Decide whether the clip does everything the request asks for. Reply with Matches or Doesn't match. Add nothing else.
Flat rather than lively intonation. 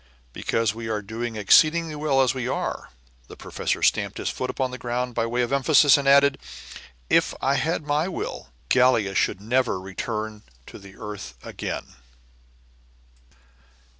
Doesn't match